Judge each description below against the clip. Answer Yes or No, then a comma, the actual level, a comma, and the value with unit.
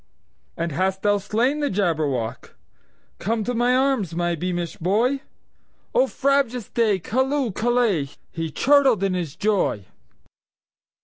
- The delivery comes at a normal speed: No, slow, 110 wpm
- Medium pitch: No, high, 205 Hz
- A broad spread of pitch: Yes, wide, 6.5 semitones